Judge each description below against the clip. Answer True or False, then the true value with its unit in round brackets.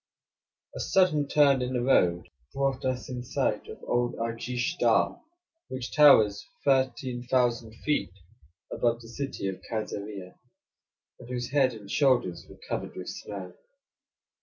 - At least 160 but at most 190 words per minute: False (135 wpm)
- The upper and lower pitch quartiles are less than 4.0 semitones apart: True (3.3 semitones)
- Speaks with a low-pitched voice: True (125 Hz)